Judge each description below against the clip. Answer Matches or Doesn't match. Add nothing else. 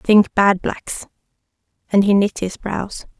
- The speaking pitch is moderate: Doesn't match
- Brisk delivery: Doesn't match